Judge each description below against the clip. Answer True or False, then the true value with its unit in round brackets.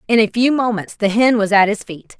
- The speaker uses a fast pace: True (275 wpm)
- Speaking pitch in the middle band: False (220 Hz)